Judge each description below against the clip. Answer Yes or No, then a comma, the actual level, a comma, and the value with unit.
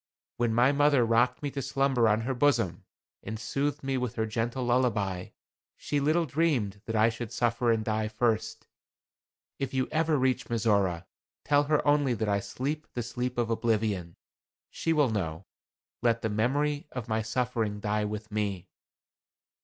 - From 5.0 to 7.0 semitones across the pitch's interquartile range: No, average, 4.0 semitones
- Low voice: Yes, low, 120 Hz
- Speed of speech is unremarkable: Yes, average, 165 wpm